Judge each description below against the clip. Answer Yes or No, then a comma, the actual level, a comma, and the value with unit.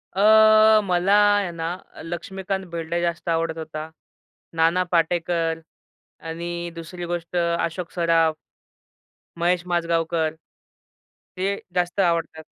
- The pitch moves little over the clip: Yes, narrow, 1.2 semitones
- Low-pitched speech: No, medium, 170 Hz